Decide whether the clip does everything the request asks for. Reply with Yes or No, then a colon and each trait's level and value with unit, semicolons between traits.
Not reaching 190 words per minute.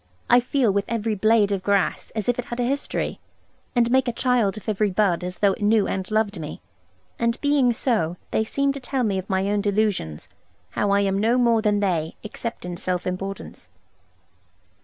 No: average, 200 wpm